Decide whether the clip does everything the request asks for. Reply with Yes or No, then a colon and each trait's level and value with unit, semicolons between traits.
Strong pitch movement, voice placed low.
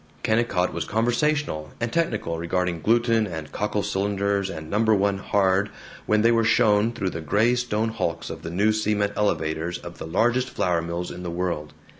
No: average, 4.7 semitones; low, 100 Hz